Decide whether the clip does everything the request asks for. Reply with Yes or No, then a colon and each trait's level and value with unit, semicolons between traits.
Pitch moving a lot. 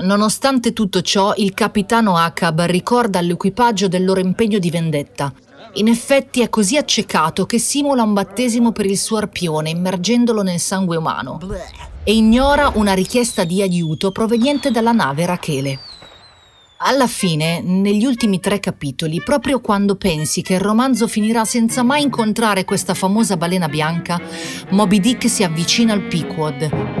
No: average, 4.9 semitones